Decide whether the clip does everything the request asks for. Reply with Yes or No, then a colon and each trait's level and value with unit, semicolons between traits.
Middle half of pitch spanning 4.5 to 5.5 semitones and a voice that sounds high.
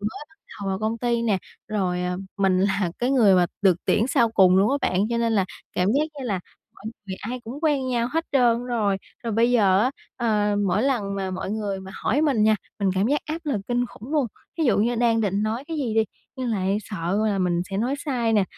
No: average, 4.0 semitones; high, 220 Hz